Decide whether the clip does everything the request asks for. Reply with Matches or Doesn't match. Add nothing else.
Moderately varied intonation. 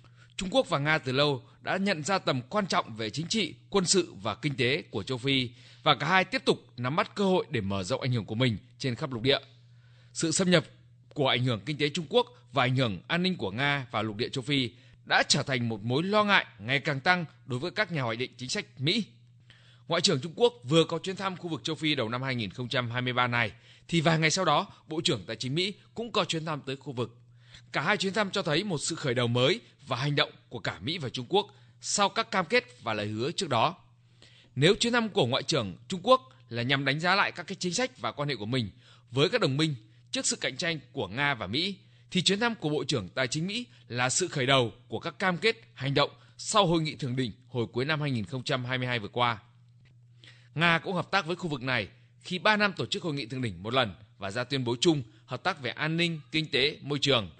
Doesn't match